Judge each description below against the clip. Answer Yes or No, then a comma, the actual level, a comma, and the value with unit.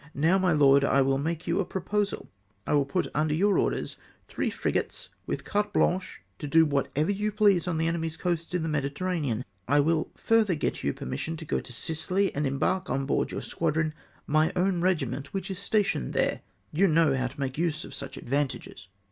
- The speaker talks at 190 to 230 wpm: Yes, average, 200 wpm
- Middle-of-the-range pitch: Yes, medium, 160 Hz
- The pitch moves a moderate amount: Yes, average, 4.7 semitones